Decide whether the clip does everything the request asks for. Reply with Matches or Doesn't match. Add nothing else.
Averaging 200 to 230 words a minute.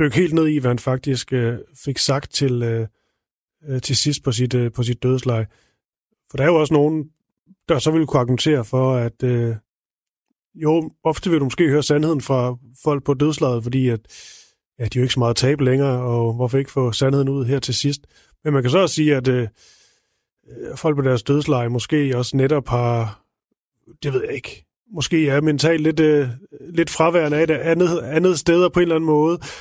Matches